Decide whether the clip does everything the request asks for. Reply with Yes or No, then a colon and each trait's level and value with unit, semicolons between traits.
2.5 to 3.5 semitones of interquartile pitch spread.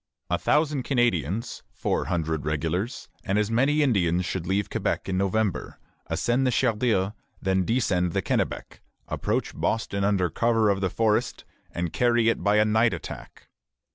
No: average, 4.3 semitones